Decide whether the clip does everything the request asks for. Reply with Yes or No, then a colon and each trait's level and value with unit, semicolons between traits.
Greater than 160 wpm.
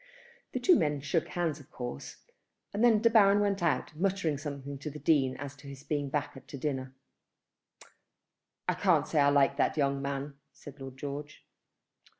Yes: average, 175 wpm